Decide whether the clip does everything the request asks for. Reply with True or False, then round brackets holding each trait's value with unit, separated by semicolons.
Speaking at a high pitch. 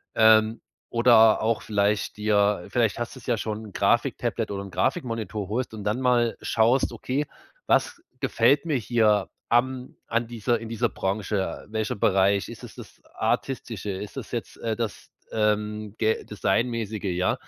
False (110 Hz)